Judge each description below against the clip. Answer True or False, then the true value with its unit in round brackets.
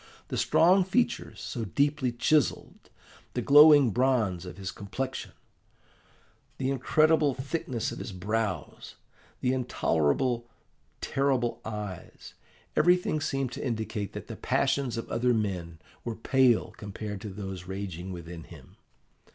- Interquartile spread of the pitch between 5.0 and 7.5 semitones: True (5.4 semitones)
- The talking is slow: True (125 wpm)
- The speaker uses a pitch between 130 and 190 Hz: False (120 Hz)